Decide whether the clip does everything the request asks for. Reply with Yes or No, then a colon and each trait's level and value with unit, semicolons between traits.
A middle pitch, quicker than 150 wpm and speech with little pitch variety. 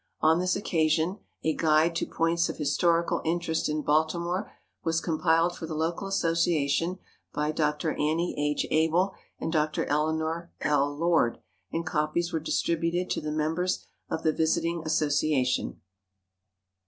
No: medium, 160 Hz; average, 140 wpm; narrow, 1.8 semitones